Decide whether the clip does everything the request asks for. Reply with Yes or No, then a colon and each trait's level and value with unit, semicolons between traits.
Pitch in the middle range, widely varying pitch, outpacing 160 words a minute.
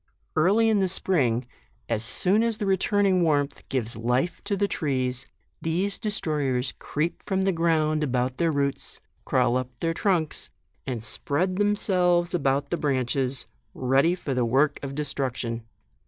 No: medium, 150 Hz; wide, 6.0 semitones; average, 155 wpm